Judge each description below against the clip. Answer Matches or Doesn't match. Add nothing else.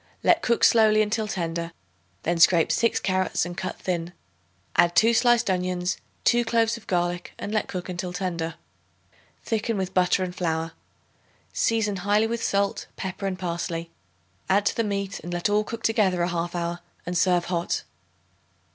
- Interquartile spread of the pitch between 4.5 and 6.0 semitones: Doesn't match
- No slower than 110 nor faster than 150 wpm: Doesn't match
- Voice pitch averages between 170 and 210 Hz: Matches